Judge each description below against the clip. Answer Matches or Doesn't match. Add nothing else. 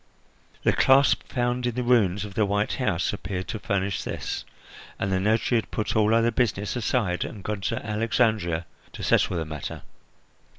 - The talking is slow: Doesn't match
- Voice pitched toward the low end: Matches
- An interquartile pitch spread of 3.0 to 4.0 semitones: Matches